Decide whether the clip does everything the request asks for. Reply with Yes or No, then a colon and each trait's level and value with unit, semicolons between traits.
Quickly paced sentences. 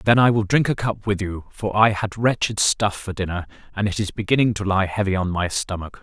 Yes: fast, 250 wpm